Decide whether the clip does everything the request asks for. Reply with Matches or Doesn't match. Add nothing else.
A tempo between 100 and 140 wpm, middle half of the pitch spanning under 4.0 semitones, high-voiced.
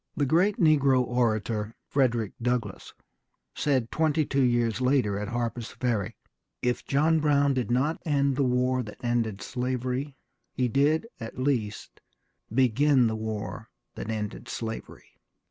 Doesn't match